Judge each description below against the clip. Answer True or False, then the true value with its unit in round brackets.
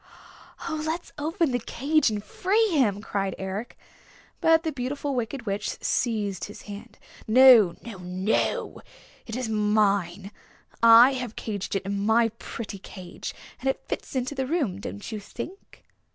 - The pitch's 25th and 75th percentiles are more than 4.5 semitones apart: True (4.9 semitones)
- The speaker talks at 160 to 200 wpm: False (150 wpm)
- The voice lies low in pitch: False (225 Hz)